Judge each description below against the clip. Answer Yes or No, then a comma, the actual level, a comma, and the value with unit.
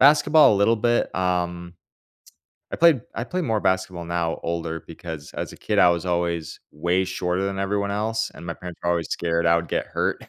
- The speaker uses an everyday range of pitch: Yes, average, 3.2 semitones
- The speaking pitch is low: Yes, very low, 90 Hz